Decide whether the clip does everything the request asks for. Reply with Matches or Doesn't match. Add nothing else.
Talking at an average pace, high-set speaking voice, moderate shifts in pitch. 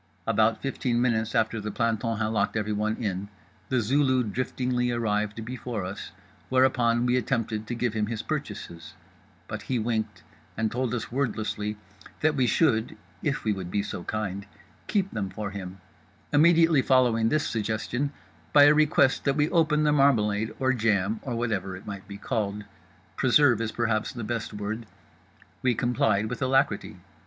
Doesn't match